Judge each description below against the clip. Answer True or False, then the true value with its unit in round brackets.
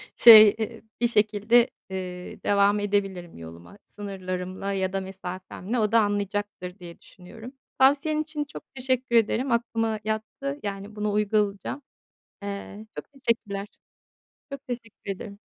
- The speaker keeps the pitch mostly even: False (3.0 semitones)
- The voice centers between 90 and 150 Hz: False (205 Hz)